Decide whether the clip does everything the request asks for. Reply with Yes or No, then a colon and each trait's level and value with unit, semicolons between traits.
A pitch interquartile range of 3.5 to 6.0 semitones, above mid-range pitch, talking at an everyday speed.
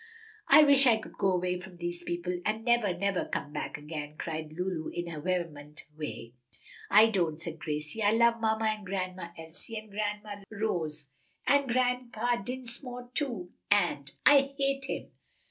Yes: wide, 5.6 semitones; high, 195 Hz; average, 165 wpm